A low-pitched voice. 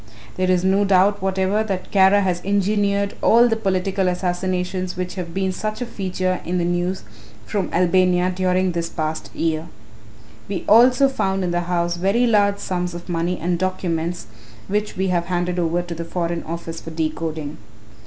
No: medium, 185 Hz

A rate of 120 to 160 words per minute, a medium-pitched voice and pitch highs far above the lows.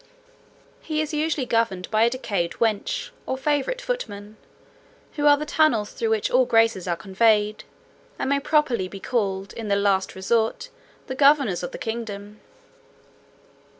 No: average, 150 wpm; high, 225 Hz; wide, 5.7 semitones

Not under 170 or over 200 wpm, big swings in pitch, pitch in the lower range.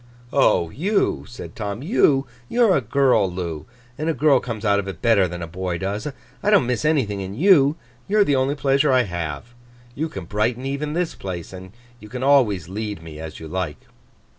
Yes: average, 195 wpm; wide, 7.0 semitones; low, 120 Hz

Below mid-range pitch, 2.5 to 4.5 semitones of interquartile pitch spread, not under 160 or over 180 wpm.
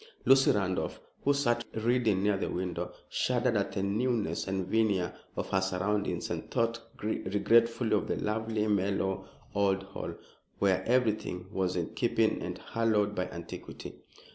No: low, 105 Hz; average, 3.2 semitones; average, 145 wpm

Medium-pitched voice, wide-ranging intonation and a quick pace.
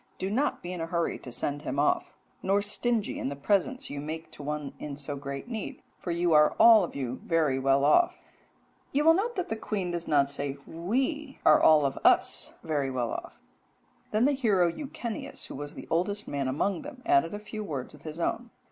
Yes: medium, 170 Hz; wide, 7.5 semitones; fast, 215 wpm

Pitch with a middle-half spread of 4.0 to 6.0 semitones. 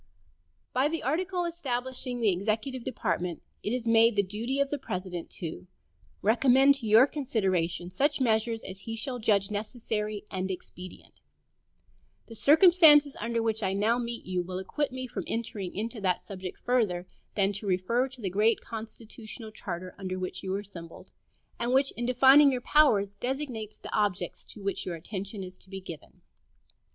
Yes: average, 4.9 semitones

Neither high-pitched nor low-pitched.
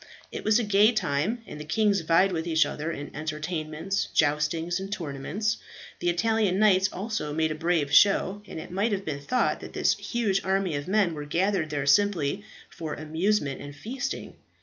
Yes: medium, 175 Hz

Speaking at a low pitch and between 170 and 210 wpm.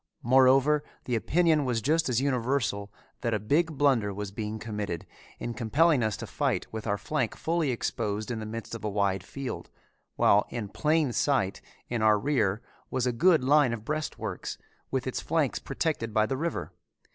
Yes: low, 120 Hz; average, 180 wpm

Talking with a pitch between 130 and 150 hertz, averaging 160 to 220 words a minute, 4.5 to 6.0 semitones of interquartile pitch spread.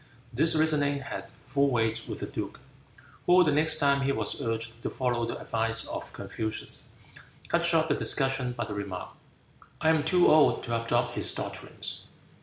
Yes: low, 135 Hz; average, 175 wpm; average, 5.2 semitones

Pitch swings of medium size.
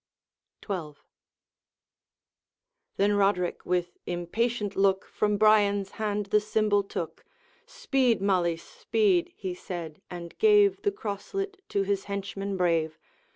Yes: average, 3.8 semitones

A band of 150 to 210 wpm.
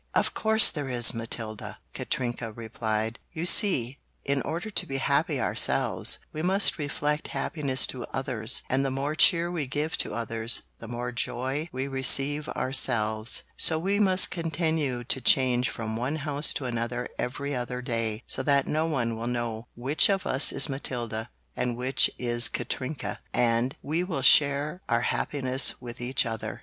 Yes: average, 165 wpm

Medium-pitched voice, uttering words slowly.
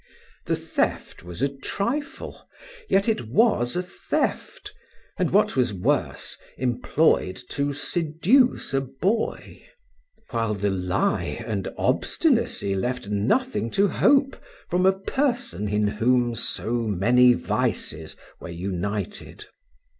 No: low, 125 Hz; slow, 115 wpm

